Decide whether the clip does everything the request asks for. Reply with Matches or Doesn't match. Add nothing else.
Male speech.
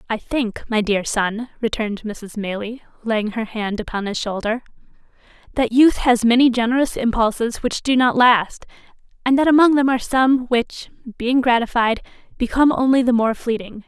Doesn't match